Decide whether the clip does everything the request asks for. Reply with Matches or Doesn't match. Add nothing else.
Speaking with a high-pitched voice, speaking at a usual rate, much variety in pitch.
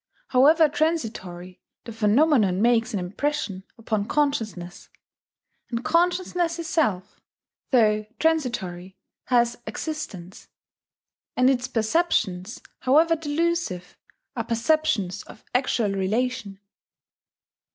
Doesn't match